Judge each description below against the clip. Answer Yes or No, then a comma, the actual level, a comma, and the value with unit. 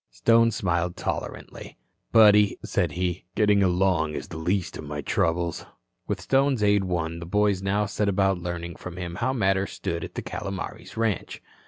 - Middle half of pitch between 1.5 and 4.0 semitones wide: Yes, average, 3.2 semitones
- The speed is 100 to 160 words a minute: No, average, 170 wpm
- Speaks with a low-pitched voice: Yes, very low, 95 Hz